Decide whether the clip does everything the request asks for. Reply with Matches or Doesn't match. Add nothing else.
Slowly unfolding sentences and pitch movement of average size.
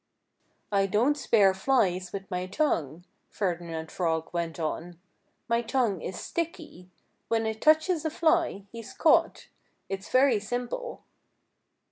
Doesn't match